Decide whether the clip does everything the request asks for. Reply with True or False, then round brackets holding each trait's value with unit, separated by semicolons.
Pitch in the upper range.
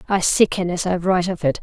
False (180 Hz)